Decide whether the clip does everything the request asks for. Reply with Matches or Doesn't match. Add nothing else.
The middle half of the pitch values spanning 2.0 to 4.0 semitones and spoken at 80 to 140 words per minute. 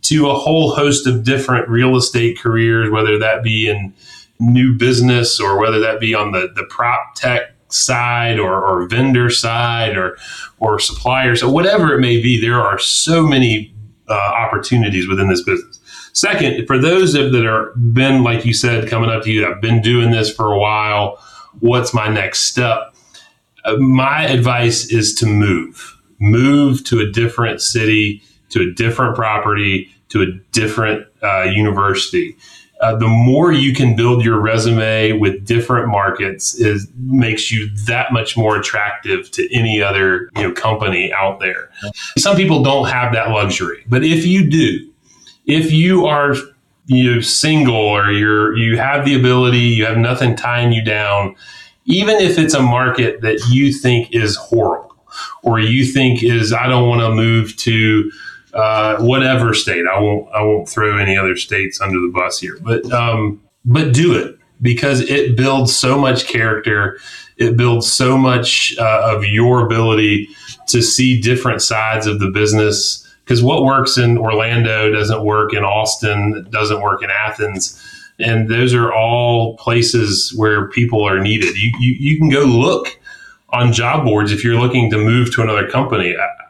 Doesn't match